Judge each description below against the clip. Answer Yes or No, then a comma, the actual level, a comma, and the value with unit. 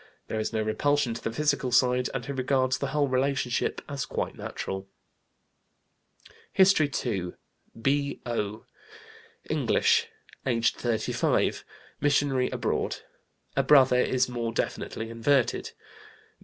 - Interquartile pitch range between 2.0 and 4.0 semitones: Yes, average, 3.4 semitones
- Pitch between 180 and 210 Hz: No, low, 130 Hz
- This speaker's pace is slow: Yes, slow, 115 wpm